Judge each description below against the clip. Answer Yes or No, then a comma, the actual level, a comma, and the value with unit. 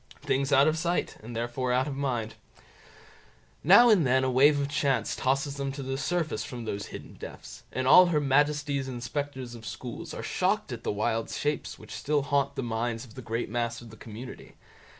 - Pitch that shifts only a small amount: No, average, 3.3 semitones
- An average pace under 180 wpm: No, average, 200 wpm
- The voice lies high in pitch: No, low, 130 Hz